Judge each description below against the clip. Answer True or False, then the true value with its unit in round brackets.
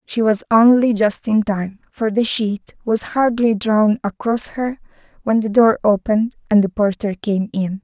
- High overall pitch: True (215 Hz)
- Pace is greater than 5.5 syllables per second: False (4.3 syllables/s)